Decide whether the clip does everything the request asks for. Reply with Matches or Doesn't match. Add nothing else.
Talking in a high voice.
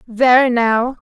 Matches